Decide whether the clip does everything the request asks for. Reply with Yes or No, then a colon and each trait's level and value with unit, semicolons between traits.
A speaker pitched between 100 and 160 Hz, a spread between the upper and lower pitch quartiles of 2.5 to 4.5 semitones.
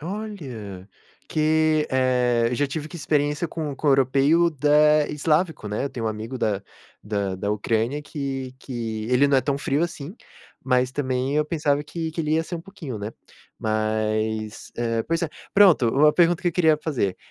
No: medium, 140 Hz; average, 5.3 semitones